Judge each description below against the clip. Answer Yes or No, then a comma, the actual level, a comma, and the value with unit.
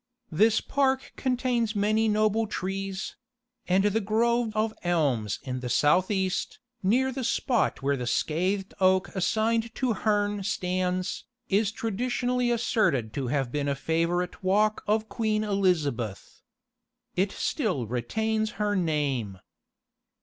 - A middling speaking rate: No, slow, 130 wpm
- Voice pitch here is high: Yes, high, 195 Hz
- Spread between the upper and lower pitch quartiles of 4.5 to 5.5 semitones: Yes, average, 5.2 semitones